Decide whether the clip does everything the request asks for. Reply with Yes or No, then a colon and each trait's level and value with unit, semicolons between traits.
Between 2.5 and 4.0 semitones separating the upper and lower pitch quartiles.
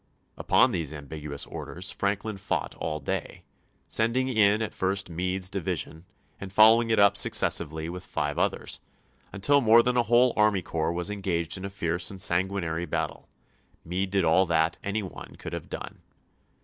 Yes: average, 3.7 semitones